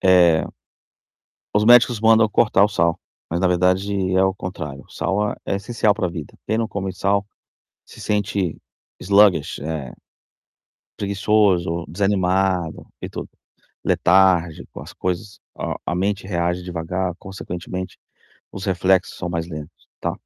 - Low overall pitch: Yes, very low, 95 Hz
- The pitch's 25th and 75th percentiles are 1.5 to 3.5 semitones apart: Yes, narrow, 2.6 semitones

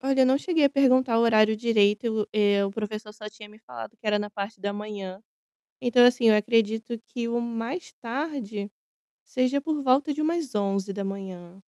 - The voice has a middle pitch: No, high, 220 Hz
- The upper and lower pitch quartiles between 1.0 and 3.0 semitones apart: No, average, 3.7 semitones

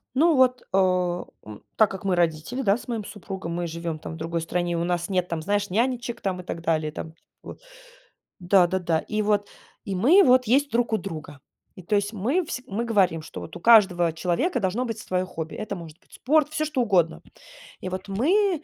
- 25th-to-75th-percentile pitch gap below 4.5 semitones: No, wide, 5.5 semitones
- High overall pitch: Yes, high, 195 Hz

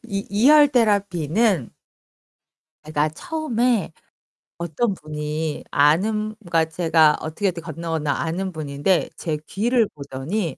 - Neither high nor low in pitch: Yes, medium, 170 Hz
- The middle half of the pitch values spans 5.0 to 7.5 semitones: Yes, wide, 5.6 semitones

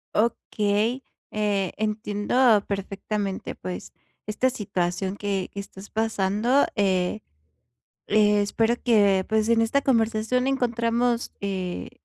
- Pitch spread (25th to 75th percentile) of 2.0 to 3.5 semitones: Yes, narrow, 2.6 semitones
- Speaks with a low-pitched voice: No, high, 210 Hz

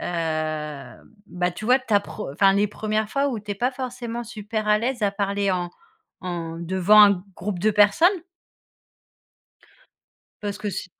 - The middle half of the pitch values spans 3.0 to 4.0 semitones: Yes, average, 3.3 semitones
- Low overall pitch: No, high, 205 Hz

